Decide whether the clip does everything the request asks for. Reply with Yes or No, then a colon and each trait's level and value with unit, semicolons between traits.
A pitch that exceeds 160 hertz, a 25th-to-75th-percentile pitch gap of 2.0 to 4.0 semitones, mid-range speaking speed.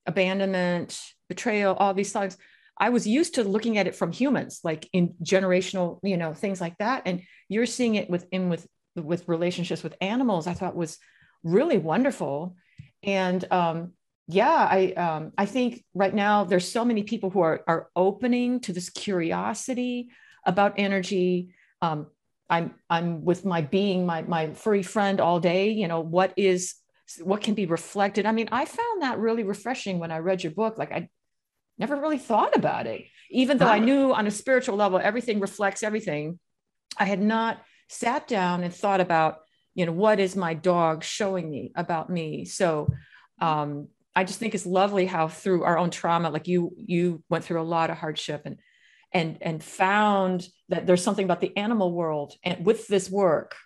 Yes: medium, 185 Hz; average, 3.6 semitones; average, 180 wpm